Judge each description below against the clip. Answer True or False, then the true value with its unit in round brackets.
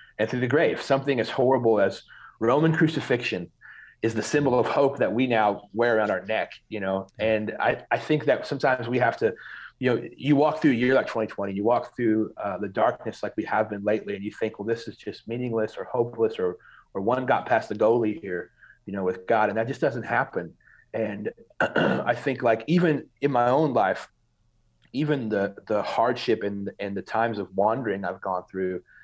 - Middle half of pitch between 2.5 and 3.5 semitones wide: False (4.5 semitones)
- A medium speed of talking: False (210 wpm)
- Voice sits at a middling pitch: False (115 Hz)